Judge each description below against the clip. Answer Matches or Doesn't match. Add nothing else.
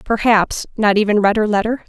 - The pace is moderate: Matches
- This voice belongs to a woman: Matches